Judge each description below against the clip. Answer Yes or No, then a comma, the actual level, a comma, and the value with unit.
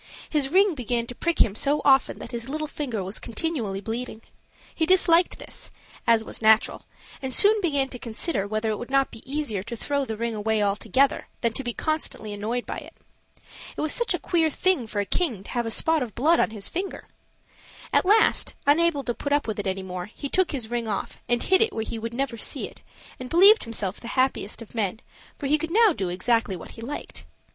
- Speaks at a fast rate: Yes, fast, 225 wpm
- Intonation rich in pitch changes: Yes, wide, 5.7 semitones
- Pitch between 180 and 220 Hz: No, high, 245 Hz